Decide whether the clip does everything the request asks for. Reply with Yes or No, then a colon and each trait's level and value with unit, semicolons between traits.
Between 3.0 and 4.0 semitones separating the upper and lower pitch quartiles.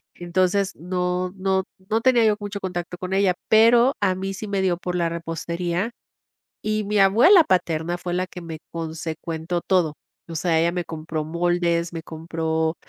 No: narrow, 2.6 semitones